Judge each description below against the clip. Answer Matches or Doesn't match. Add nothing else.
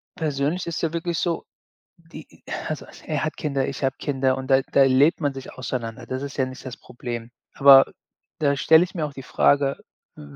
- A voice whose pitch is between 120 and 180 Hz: Matches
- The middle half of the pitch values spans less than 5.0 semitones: Matches